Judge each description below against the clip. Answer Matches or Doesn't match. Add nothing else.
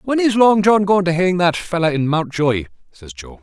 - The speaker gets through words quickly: Matches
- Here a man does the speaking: Matches